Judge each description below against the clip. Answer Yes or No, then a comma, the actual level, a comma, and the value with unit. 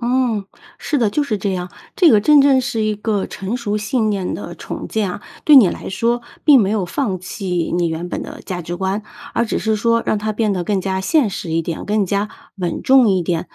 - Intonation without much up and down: No, average, 3.9 semitones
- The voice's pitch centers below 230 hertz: Yes, high, 210 Hz